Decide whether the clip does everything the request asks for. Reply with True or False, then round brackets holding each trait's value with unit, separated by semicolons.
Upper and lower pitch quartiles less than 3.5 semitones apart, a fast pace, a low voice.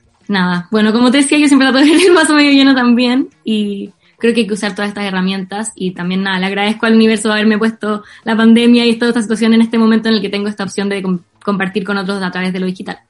False (2.8 semitones; 270 wpm; 215 Hz)